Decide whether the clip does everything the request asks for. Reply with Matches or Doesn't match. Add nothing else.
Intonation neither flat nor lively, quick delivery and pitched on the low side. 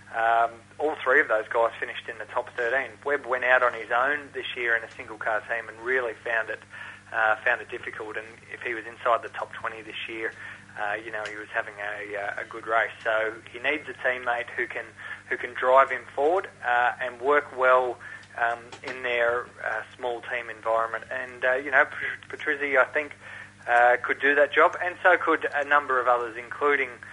Doesn't match